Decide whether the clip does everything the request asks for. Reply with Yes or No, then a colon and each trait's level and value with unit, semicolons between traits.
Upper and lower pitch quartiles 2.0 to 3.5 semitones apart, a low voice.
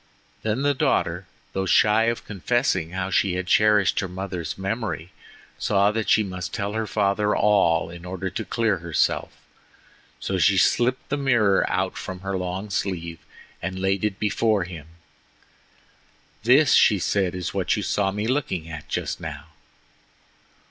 Yes: average, 3.0 semitones; very low, 95 Hz